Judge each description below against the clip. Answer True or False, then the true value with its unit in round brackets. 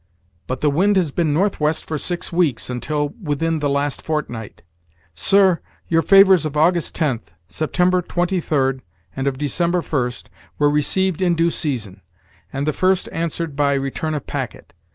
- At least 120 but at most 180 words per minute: True (155 wpm)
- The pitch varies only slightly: False (3.8 semitones)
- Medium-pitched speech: True (155 Hz)